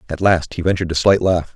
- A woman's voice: No, male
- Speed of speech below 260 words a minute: No, fast, 270 wpm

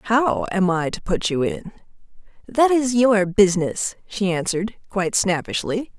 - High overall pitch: Yes, high, 205 Hz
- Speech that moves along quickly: No, average, 150 wpm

